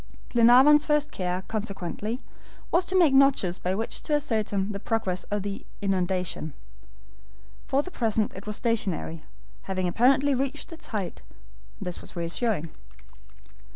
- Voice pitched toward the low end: No, high, 215 Hz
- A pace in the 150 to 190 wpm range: No, slow, 135 wpm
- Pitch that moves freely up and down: Yes, wide, 6.3 semitones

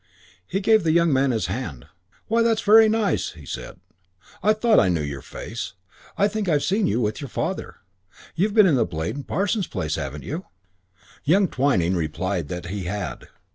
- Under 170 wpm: No, average, 185 wpm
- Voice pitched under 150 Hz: Yes, low, 135 Hz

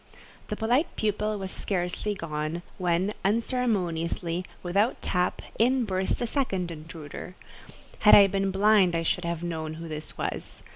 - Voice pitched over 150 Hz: Yes, medium, 185 Hz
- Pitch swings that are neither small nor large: Yes, average, 3.9 semitones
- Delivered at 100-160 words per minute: Yes, average, 145 wpm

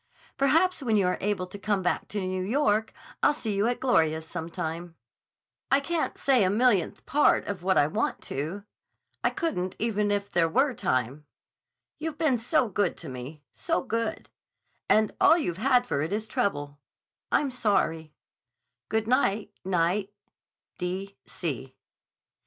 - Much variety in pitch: Yes, wide, 6.2 semitones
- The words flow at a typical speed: Yes, average, 150 wpm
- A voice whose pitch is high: Yes, high, 205 Hz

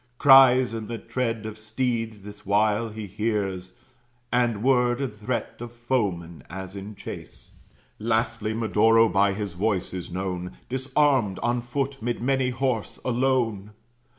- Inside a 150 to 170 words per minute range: No, average, 140 wpm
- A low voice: Yes, low, 115 Hz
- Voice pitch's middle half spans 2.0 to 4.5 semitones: Yes, average, 3.2 semitones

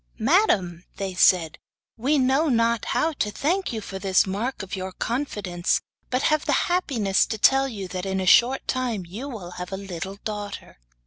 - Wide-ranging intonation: Yes, wide, 5.7 semitones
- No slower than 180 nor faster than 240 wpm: Yes, average, 185 wpm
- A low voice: No, high, 210 Hz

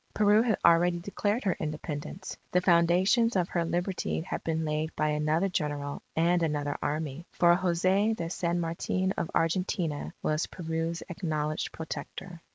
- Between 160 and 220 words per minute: No, average, 150 wpm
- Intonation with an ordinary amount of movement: Yes, average, 3.0 semitones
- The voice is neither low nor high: Yes, medium, 170 Hz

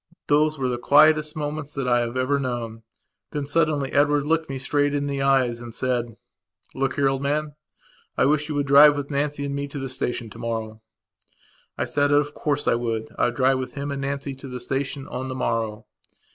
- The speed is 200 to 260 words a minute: Yes, fast, 205 wpm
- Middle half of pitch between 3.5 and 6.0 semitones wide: No, narrow, 2.5 semitones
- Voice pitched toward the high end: No, medium, 140 Hz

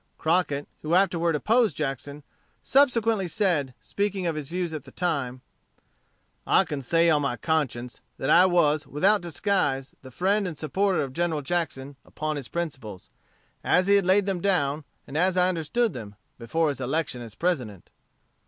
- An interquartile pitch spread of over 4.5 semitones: Yes, average, 4.9 semitones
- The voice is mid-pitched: Yes, medium, 160 Hz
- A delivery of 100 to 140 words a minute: No, average, 165 wpm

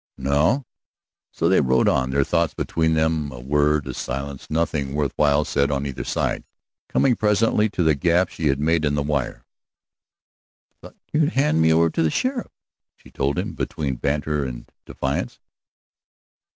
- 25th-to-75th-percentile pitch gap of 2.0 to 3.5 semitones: Yes, average, 3.0 semitones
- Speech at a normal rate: Yes, average, 170 wpm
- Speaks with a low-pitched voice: Yes, very low, 75 Hz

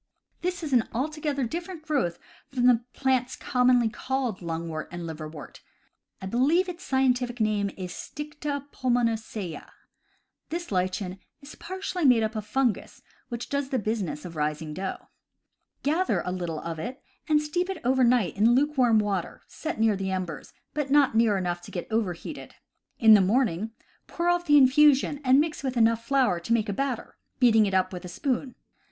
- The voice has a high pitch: Yes, high, 240 Hz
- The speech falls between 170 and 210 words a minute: Yes, average, 180 wpm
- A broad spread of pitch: Yes, wide, 6.6 semitones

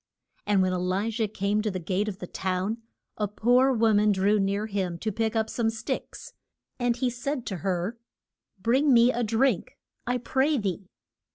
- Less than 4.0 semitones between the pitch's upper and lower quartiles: Yes, average, 3.5 semitones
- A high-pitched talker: Yes, high, 215 Hz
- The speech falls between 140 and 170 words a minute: No, average, 190 wpm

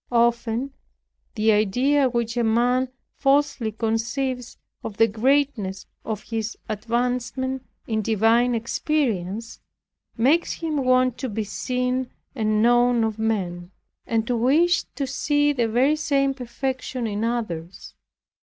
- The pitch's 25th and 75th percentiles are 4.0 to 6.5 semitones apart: No, average, 2.9 semitones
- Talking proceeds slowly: Yes, slow, 125 wpm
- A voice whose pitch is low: No, high, 240 Hz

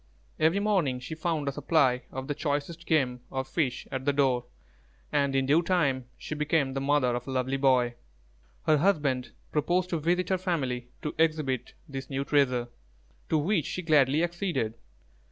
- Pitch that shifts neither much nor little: Yes, average, 3.7 semitones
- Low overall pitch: No, medium, 145 Hz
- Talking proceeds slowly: No, average, 170 wpm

